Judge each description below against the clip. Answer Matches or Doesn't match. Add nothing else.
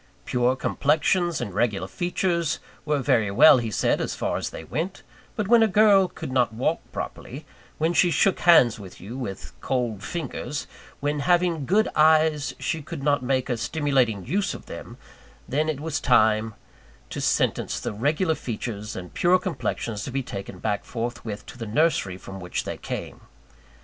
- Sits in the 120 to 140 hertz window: Matches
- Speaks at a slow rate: Doesn't match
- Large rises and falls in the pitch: Matches